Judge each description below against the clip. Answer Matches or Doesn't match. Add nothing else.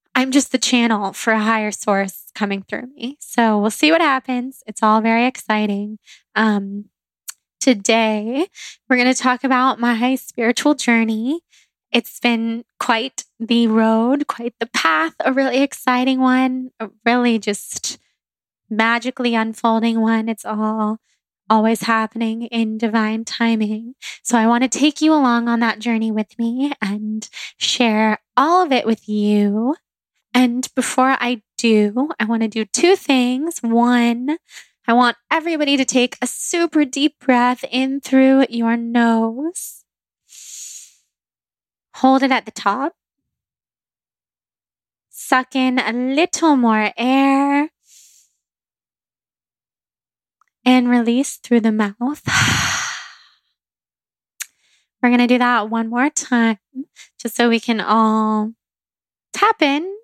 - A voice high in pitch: Matches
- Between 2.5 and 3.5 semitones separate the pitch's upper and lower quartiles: Matches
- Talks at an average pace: Doesn't match